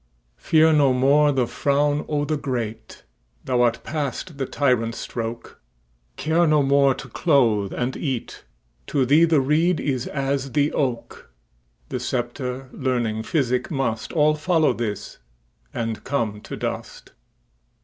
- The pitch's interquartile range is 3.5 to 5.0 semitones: Yes, average, 4.4 semitones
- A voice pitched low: Yes, low, 130 Hz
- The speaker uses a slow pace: Yes, slow, 120 wpm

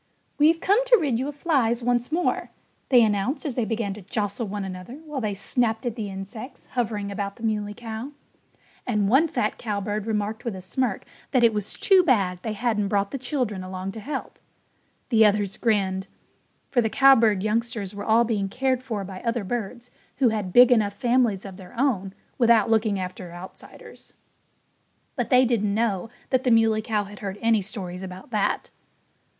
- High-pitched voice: Yes, high, 220 Hz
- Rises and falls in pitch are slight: No, average, 3.6 semitones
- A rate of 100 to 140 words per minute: No, average, 185 wpm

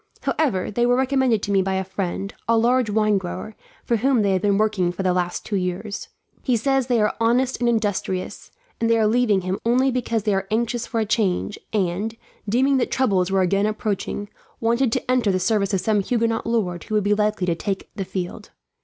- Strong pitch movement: No, average, 3.5 semitones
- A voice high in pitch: Yes, high, 215 Hz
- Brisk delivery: Yes, fast, 215 wpm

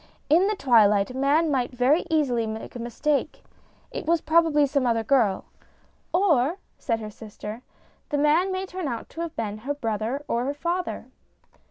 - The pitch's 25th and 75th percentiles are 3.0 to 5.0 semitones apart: No, wide, 5.6 semitones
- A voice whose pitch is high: Yes, very high, 275 Hz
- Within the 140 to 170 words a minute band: No, average, 185 wpm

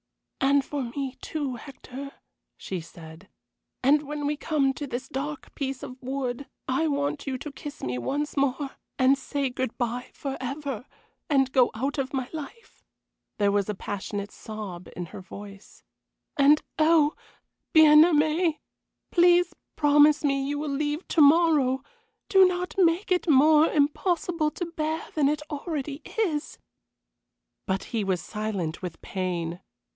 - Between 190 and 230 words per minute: No, average, 150 wpm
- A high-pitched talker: Yes, very high, 280 Hz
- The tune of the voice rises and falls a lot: No, average, 3.7 semitones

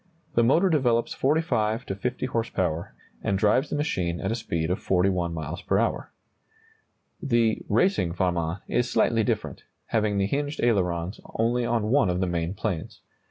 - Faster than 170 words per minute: No, average, 165 wpm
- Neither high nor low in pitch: No, low, 105 Hz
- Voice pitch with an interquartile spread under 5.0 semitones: No, average, 5.3 semitones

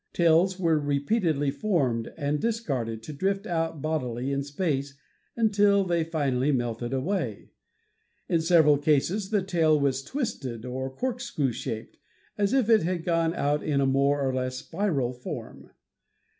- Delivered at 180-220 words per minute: No, average, 155 wpm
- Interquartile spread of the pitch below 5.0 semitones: No, wide, 5.5 semitones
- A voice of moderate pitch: Yes, medium, 150 Hz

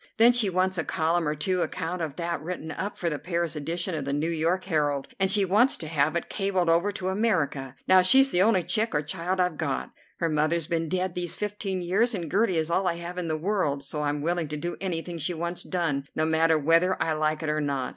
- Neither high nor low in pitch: Yes, medium, 170 Hz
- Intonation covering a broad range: No, average, 3.2 semitones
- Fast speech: Yes, fast, 245 wpm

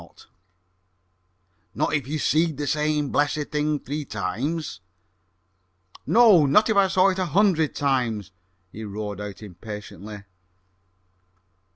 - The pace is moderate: No, slow, 115 wpm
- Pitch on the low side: No, medium, 145 Hz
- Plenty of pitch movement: Yes, wide, 7.0 semitones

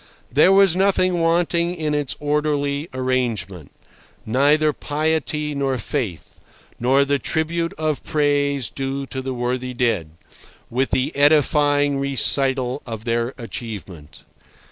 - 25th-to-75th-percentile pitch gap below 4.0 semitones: Yes, average, 3.2 semitones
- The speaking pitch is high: No, medium, 140 Hz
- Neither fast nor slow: No, slow, 115 wpm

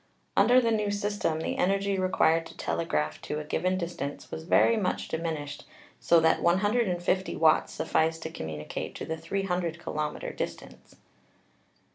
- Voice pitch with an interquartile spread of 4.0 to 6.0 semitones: No, average, 3.5 semitones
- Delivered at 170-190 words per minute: No, average, 145 wpm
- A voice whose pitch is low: No, medium, 170 Hz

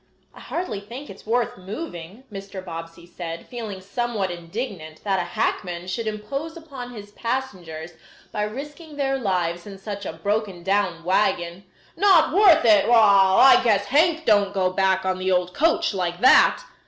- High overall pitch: Yes, high, 200 Hz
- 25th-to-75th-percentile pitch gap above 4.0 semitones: Yes, average, 5.2 semitones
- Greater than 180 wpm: No, average, 165 wpm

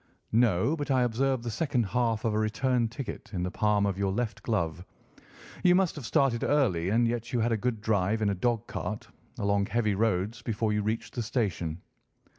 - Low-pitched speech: Yes, low, 110 Hz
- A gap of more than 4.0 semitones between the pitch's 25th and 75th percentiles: No, average, 3.1 semitones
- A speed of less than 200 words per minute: No, fast, 205 wpm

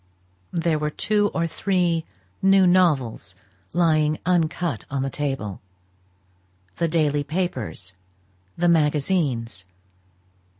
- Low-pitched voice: No, medium, 155 Hz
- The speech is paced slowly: Yes, slow, 95 wpm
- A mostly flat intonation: No, average, 4.1 semitones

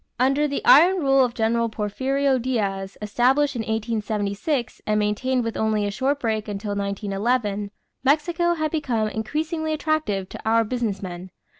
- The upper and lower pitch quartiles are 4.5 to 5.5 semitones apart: Yes, average, 4.9 semitones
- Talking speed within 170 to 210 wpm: No, average, 150 wpm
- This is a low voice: No, high, 230 Hz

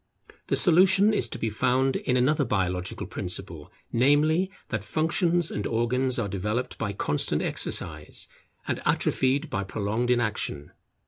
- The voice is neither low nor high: No, low, 125 Hz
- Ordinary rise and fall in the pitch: No, wide, 6.3 semitones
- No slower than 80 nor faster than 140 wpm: Yes, slow, 135 wpm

